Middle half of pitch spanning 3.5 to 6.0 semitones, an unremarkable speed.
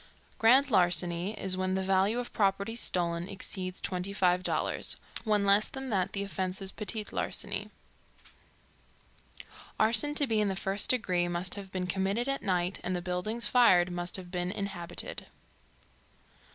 No: average, 2.8 semitones; average, 150 wpm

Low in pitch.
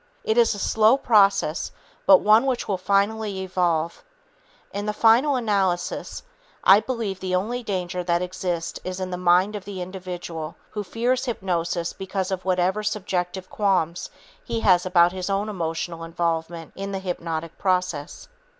No: medium, 185 Hz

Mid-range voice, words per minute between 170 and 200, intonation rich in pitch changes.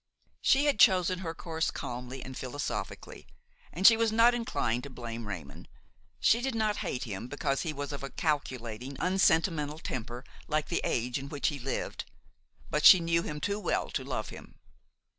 Yes: medium, 150 Hz; average, 180 wpm; wide, 6.6 semitones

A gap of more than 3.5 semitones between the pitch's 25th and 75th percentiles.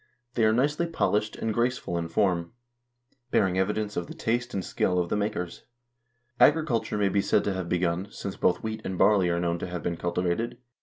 Yes: average, 4.0 semitones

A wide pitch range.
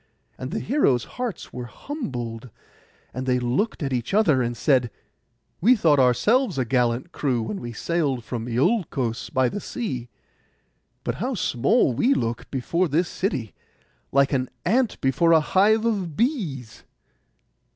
Yes: wide, 8.4 semitones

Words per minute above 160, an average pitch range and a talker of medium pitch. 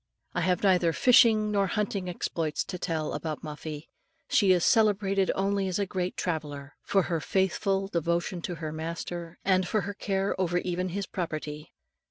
Yes: average, 175 wpm; average, 3.0 semitones; medium, 180 Hz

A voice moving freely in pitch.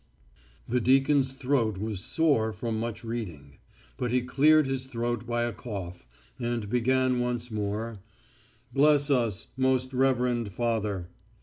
No: average, 3.0 semitones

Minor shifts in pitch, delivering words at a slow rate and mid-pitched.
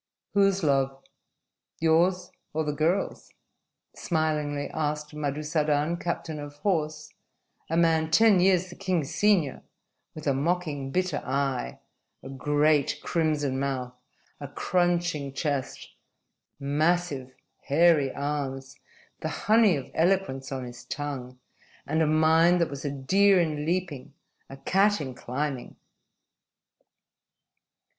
No: average, 3.8 semitones; slow, 115 wpm; medium, 150 Hz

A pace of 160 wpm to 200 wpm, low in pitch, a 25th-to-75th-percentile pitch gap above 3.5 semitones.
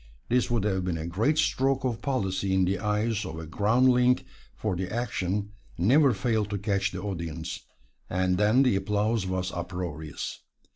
Yes: average, 165 wpm; low, 100 Hz; average, 4.2 semitones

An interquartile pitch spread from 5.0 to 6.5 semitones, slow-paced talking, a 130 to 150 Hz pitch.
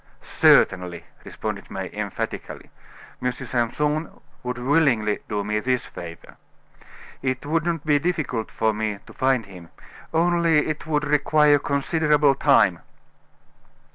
Yes: wide, 5.5 semitones; slow, 120 wpm; medium, 140 Hz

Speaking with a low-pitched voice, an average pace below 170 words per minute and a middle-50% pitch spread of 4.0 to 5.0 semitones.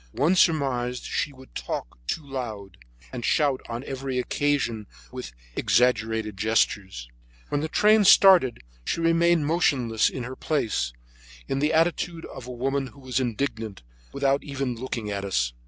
Yes: low, 130 Hz; average, 155 wpm; average, 4.5 semitones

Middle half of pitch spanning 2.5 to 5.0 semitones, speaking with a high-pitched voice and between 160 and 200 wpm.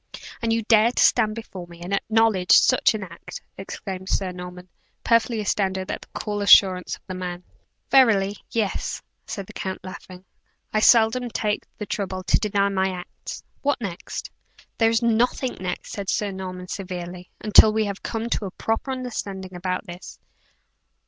Yes: average, 3.2 semitones; high, 200 Hz; average, 170 wpm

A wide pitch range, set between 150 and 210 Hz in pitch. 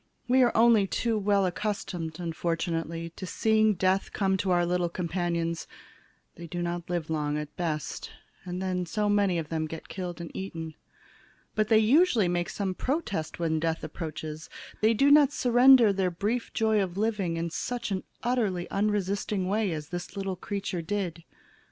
No: average, 4.0 semitones; medium, 185 Hz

